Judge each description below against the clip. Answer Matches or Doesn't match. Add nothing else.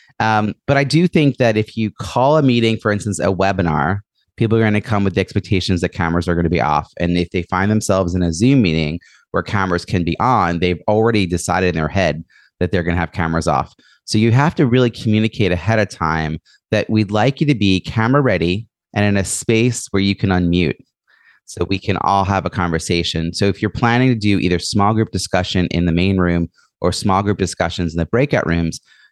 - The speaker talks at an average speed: Doesn't match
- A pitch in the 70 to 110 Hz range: Matches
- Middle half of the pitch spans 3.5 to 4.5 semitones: Matches